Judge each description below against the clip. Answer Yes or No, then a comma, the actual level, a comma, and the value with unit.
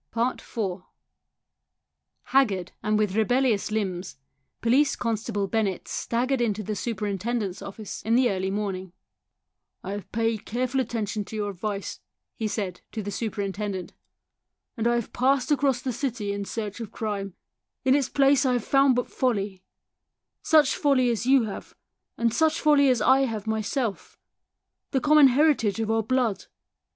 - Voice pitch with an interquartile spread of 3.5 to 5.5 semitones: Yes, average, 4.0 semitones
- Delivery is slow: No, average, 155 wpm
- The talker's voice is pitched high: Yes, high, 225 Hz